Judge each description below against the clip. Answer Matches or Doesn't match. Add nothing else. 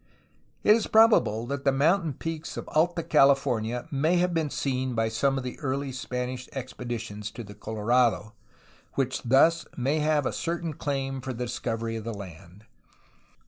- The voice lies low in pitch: Matches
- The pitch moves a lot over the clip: Doesn't match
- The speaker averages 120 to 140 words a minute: Doesn't match